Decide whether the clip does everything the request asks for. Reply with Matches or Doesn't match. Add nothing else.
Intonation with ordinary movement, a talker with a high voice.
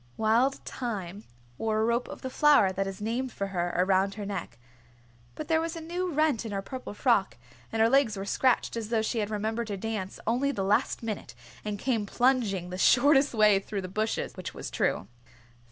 Matches